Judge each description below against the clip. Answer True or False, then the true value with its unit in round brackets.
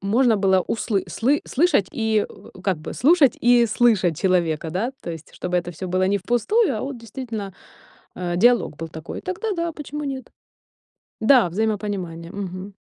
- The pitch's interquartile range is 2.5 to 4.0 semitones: False (5.3 semitones)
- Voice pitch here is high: True (210 Hz)